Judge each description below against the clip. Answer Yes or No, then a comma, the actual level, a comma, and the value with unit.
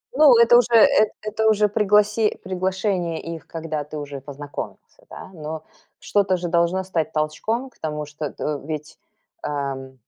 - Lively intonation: Yes, wide, 5.7 semitones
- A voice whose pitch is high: No, medium, 170 Hz